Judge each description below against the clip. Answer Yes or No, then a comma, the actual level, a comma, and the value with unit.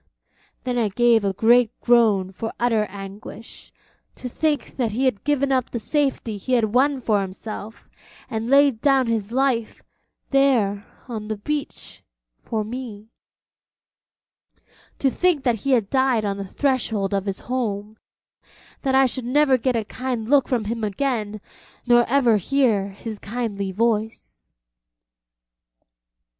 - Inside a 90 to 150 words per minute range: Yes, average, 145 wpm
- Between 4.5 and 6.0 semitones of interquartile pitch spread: No, average, 3.7 semitones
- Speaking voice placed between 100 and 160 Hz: No, high, 230 Hz